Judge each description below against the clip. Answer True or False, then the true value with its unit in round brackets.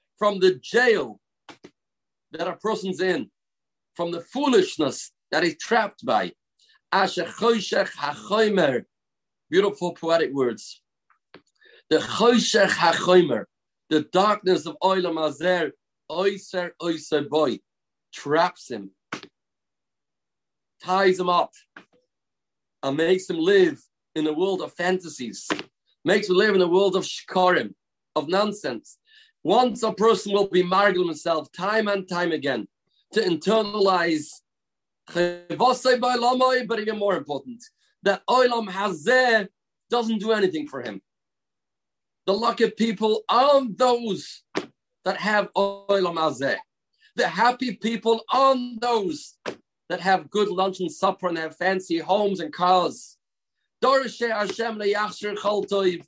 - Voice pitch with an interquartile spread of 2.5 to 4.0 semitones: False (4.6 semitones)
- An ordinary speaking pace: False (105 wpm)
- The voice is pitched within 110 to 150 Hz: False (200 Hz)